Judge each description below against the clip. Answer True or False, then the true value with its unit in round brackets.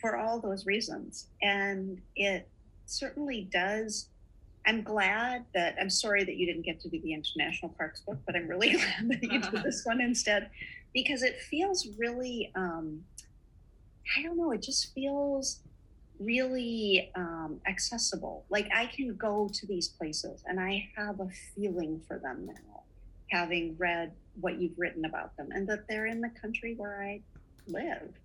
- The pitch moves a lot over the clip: False (4.4 semitones)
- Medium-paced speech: True (165 wpm)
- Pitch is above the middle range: True (205 Hz)